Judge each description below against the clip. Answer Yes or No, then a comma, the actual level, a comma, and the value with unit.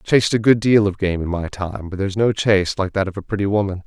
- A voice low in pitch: Yes, low, 100 Hz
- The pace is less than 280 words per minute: No, fast, 310 wpm